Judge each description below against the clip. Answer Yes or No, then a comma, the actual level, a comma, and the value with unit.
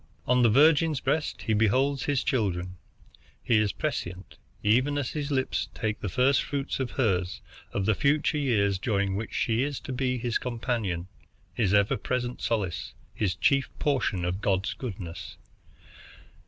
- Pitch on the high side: No, low, 115 Hz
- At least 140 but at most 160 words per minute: Yes, average, 155 wpm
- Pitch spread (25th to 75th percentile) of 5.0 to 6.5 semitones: Yes, average, 5.3 semitones